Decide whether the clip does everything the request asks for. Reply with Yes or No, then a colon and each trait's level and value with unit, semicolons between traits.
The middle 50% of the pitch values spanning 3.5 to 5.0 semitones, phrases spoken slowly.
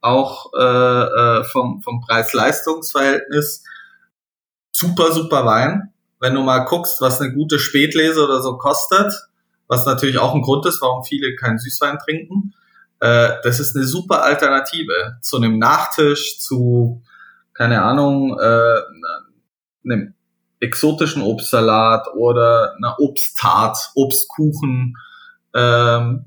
Yes: average, 4.6 semitones; slow, 120 wpm